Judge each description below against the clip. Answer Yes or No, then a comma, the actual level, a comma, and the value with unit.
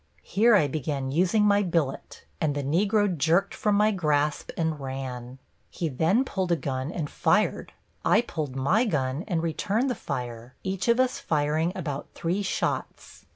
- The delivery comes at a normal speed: Yes, average, 165 wpm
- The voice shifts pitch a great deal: Yes, wide, 6.0 semitones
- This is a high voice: No, medium, 165 Hz